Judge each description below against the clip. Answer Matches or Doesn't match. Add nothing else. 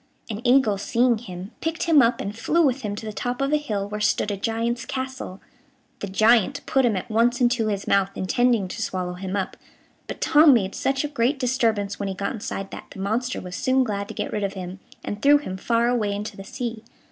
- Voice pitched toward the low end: Doesn't match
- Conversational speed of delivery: Doesn't match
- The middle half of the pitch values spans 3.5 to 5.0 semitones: Matches